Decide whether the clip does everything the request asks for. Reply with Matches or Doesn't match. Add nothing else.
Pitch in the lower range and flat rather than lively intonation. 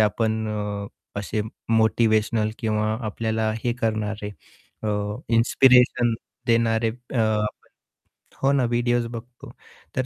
Matches